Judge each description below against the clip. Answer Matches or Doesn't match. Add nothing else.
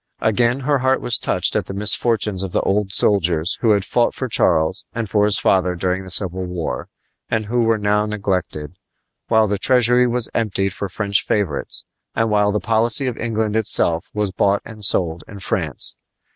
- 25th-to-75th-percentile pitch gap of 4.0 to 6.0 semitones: Doesn't match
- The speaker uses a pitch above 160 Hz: Doesn't match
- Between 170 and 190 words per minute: Matches